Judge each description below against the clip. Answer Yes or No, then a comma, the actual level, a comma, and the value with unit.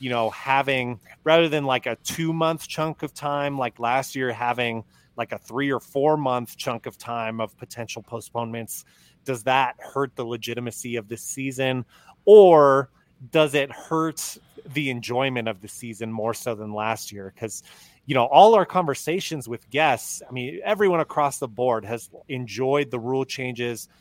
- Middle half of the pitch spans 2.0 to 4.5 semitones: Yes, average, 3.9 semitones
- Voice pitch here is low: Yes, low, 130 Hz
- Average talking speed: Yes, average, 170 wpm